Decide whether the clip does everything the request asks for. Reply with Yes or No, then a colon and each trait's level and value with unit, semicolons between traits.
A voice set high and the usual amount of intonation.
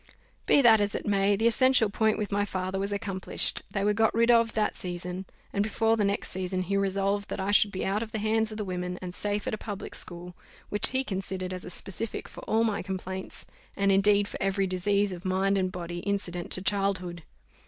No: high, 200 Hz; narrow, 2.0 semitones